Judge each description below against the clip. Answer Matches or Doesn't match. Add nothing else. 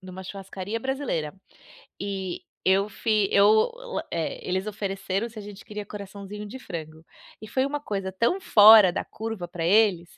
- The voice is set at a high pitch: Matches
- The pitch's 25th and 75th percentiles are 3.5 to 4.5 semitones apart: Doesn't match